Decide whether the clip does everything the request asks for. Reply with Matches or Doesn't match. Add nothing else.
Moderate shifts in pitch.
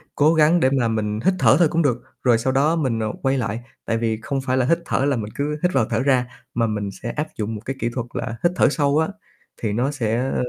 Matches